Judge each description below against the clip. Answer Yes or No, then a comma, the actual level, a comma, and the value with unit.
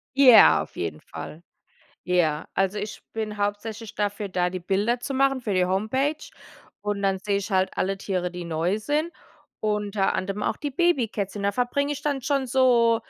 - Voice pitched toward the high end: Yes, high, 210 Hz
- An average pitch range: Yes, average, 4.6 semitones